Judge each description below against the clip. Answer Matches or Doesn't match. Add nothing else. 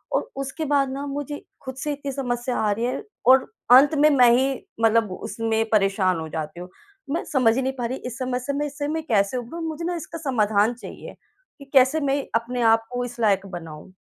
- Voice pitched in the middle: Doesn't match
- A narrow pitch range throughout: Doesn't match